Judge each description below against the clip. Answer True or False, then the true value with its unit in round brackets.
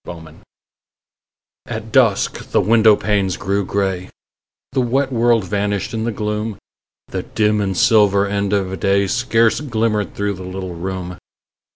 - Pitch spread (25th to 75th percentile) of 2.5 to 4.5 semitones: True (2.8 semitones)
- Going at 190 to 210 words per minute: False (145 wpm)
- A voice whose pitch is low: True (105 Hz)